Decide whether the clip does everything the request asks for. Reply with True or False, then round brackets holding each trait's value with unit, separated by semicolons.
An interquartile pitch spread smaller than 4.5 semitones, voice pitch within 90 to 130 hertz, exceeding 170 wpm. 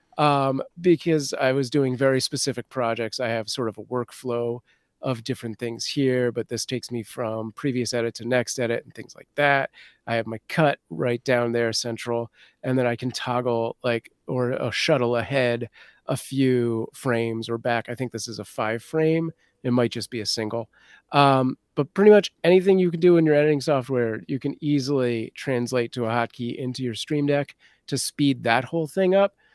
True (3.3 semitones; 125 Hz; 195 wpm)